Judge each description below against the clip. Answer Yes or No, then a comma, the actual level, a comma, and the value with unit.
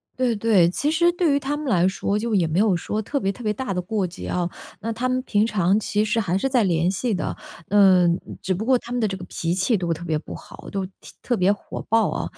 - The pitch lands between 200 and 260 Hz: Yes, high, 205 Hz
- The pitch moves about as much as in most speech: Yes, average, 4.5 semitones